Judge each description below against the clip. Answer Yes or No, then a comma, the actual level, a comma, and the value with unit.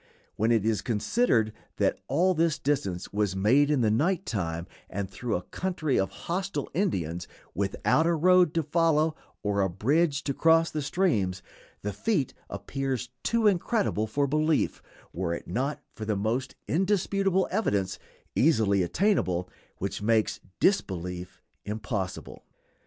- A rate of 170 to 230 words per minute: No, average, 140 wpm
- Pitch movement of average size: No, wide, 8.8 semitones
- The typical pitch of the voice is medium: No, low, 130 Hz